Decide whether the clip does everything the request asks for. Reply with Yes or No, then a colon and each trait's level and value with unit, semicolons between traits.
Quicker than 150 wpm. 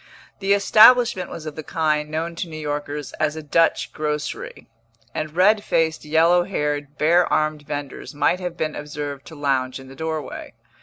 Yes: average, 170 wpm